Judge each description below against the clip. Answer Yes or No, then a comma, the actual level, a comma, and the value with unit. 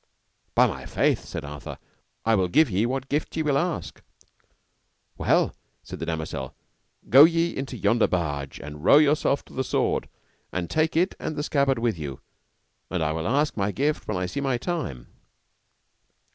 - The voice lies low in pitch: Yes, low, 120 Hz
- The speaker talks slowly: No, average, 175 wpm